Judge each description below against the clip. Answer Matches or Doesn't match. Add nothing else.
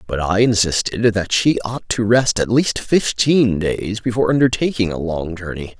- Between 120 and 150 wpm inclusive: Doesn't match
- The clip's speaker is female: Doesn't match